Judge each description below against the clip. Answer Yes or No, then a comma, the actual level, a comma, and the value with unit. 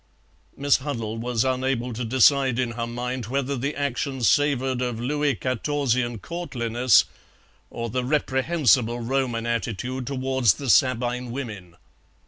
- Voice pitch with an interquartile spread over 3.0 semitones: No, narrow, 2.4 semitones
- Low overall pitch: Yes, low, 125 Hz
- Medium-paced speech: No, slow, 125 wpm